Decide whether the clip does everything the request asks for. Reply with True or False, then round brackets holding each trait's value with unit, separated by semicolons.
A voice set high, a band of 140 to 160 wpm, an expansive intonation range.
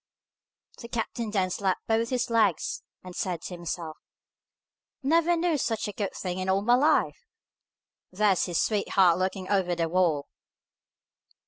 False (195 Hz; 145 wpm; 4.2 semitones)